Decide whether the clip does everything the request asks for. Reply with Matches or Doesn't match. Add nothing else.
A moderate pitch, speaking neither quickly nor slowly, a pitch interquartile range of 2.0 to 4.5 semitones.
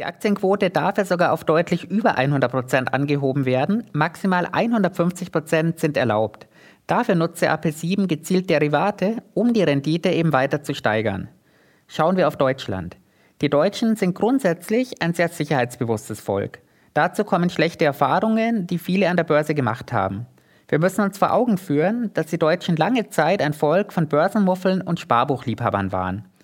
Doesn't match